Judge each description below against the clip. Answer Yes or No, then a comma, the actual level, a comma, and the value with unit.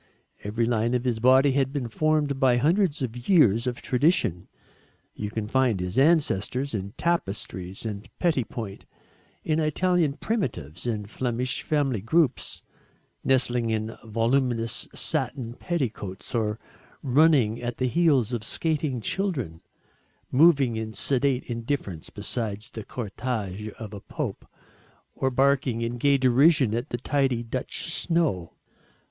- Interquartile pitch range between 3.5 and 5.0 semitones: Yes, average, 4.2 semitones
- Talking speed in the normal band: No, slow, 130 wpm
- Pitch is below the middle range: Yes, low, 125 Hz